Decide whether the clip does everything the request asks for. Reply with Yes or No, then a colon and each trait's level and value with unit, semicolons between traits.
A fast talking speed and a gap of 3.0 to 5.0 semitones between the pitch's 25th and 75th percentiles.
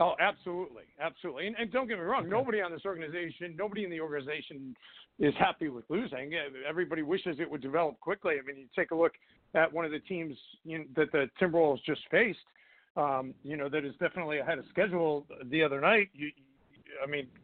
Yes: fast, 210 wpm; average, 3.7 semitones